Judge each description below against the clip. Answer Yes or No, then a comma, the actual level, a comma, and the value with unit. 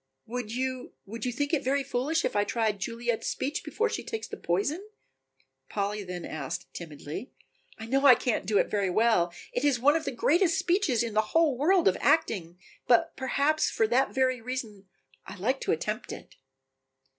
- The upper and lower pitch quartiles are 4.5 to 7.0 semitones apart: Yes, average, 5.2 semitones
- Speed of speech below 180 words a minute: No, average, 190 wpm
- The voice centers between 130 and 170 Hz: No, high, 245 Hz